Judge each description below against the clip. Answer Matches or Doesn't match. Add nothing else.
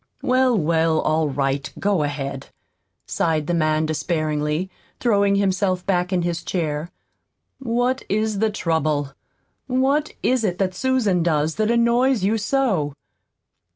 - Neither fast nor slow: Doesn't match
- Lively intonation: Matches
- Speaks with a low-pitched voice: Doesn't match